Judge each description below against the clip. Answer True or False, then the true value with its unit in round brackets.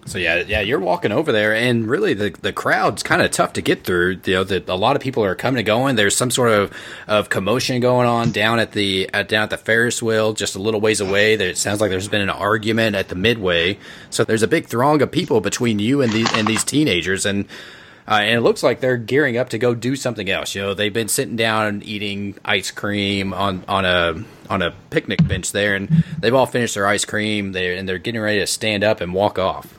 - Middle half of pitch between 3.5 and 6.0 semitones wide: False (2.9 semitones)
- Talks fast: True (250 wpm)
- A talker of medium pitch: False (105 Hz)